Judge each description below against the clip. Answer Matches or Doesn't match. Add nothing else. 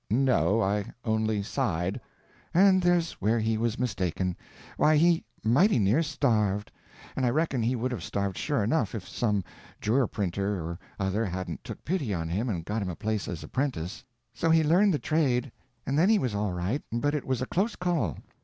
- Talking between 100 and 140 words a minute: Doesn't match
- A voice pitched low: Matches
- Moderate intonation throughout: Doesn't match